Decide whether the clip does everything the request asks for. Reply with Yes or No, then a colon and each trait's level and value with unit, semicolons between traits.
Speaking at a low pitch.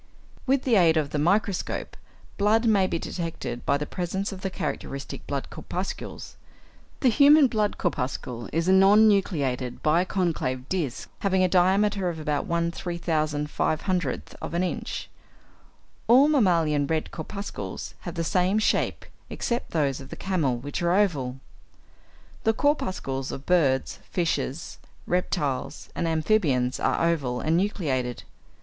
No: medium, 170 Hz